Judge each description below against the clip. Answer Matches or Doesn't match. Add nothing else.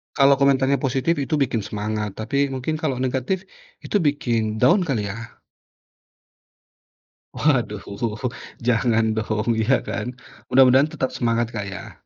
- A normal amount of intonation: Matches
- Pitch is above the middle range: Doesn't match